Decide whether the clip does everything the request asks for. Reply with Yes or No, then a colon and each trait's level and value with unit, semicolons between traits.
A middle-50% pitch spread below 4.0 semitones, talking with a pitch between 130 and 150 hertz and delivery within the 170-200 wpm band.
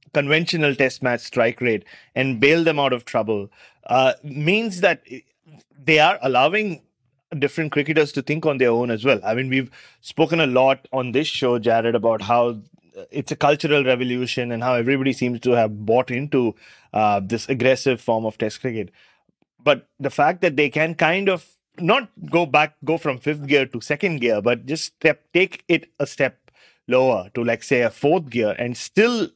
No: average, 4.3 semitones; low, 135 Hz; average, 185 wpm